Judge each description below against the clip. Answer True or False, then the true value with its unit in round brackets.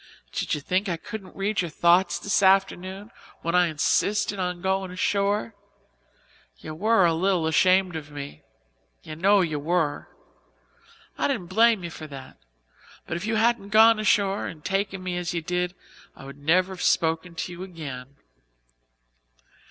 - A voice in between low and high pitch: True (180 Hz)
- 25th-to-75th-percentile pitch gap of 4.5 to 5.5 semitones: False (3.2 semitones)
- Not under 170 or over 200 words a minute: False (160 wpm)